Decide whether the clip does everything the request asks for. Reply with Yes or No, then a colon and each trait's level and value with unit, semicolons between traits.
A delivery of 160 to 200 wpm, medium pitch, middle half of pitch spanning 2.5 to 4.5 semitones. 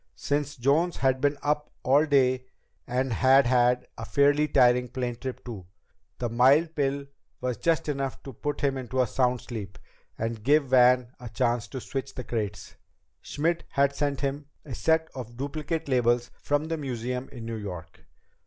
No: average, 170 wpm; low, 130 Hz; average, 2.8 semitones